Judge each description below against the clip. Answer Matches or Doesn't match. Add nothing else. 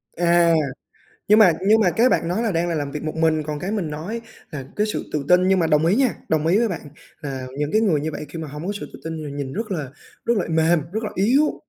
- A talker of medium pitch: Matches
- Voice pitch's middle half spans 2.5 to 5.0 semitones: Doesn't match